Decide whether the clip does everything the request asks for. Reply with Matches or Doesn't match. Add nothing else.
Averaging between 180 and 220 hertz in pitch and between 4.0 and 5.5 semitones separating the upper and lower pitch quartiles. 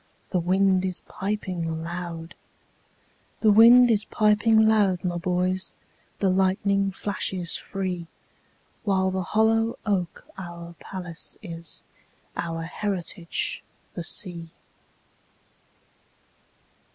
Doesn't match